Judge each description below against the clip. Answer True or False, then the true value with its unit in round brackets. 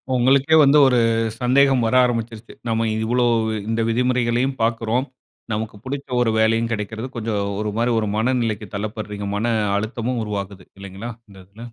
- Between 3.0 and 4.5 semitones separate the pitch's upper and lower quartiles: False (2.5 semitones)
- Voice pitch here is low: True (115 Hz)